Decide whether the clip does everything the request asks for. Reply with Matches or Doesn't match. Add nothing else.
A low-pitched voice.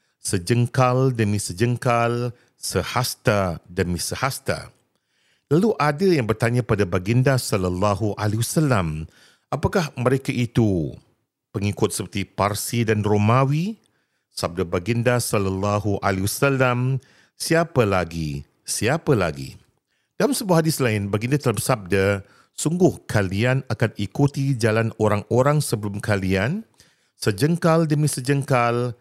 Matches